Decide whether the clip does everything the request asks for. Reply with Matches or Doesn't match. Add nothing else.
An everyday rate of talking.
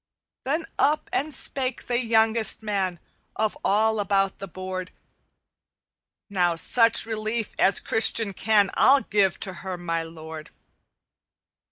Doesn't match